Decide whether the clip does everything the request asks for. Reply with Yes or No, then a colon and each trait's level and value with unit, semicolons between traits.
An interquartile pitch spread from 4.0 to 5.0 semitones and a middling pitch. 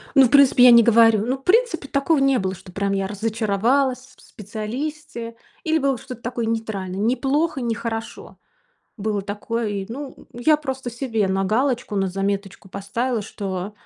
No: average, 4.7 semitones; high, 230 Hz